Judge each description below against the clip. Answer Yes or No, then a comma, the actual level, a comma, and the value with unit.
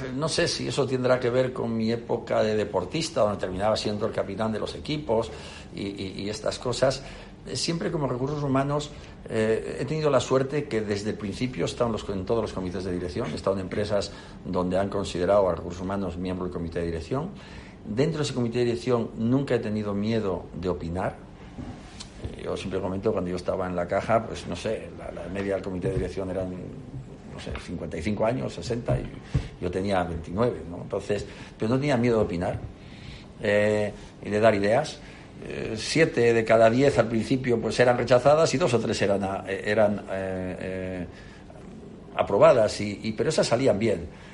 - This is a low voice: Yes, low, 105 Hz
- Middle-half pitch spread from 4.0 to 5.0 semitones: Yes, average, 4.6 semitones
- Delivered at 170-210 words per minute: Yes, fast, 190 wpm